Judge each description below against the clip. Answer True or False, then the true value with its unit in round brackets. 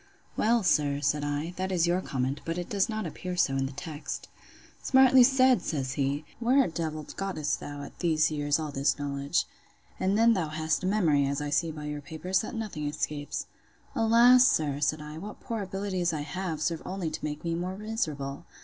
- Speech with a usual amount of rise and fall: True (4.8 semitones)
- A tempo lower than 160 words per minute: False (205 wpm)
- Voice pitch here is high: False (160 Hz)